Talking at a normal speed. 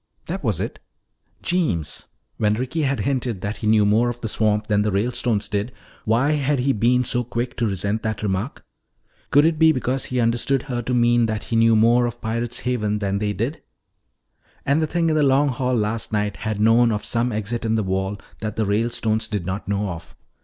No: fast, 210 wpm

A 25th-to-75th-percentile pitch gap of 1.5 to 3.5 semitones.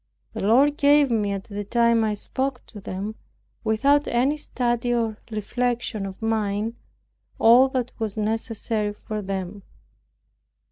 Yes: average, 2.9 semitones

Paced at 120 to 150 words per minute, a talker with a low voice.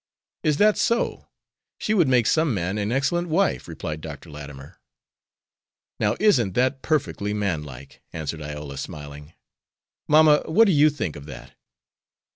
Yes: average, 140 wpm; low, 105 Hz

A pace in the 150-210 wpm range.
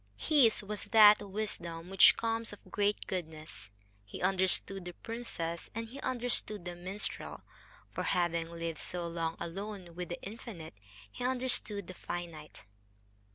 No: average, 140 wpm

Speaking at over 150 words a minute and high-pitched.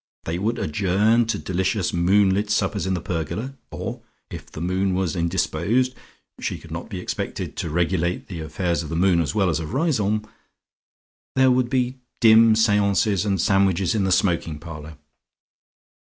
No: average, 165 wpm; very low, 95 Hz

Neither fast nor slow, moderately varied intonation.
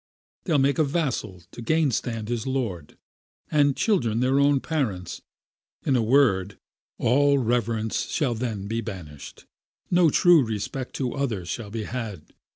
Yes: average, 150 wpm; average, 4.6 semitones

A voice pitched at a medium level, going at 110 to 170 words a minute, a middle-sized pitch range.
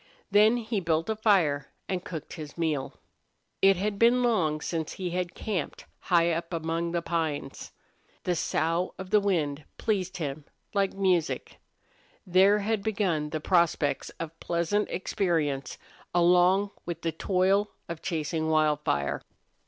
Yes: medium, 175 Hz; average, 145 wpm; average, 3.6 semitones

